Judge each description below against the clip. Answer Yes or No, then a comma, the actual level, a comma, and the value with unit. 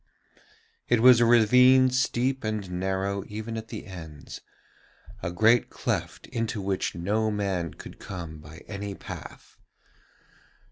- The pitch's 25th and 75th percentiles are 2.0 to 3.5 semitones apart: No, average, 3.9 semitones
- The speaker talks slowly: Yes, slow, 130 wpm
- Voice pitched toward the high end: No, low, 105 Hz